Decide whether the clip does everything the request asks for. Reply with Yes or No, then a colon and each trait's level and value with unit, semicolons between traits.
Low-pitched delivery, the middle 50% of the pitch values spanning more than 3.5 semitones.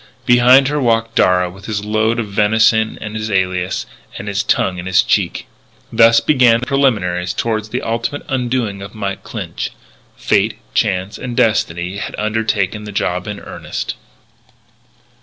No: low, 110 Hz; average, 3.1 semitones